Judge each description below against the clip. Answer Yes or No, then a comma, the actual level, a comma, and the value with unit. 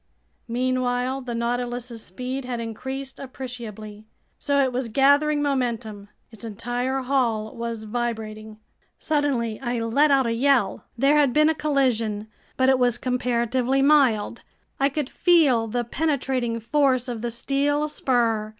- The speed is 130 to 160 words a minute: Yes, average, 140 wpm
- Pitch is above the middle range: Yes, high, 245 Hz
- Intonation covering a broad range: No, average, 3.0 semitones